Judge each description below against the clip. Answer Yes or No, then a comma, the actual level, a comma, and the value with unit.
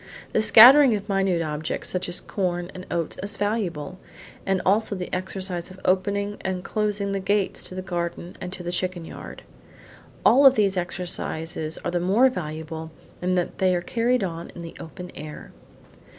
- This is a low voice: No, medium, 185 Hz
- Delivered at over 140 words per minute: Yes, average, 180 wpm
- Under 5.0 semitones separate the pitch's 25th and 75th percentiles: Yes, narrow, 2.6 semitones